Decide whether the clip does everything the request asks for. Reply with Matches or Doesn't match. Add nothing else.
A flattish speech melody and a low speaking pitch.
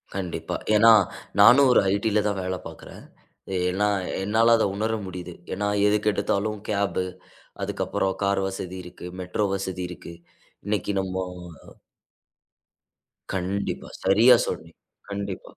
Matches